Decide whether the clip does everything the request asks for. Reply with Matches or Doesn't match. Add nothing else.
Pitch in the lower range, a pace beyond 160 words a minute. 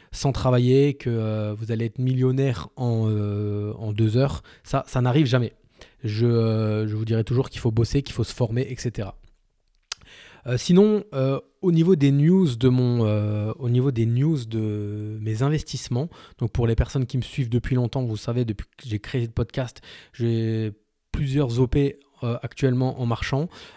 Matches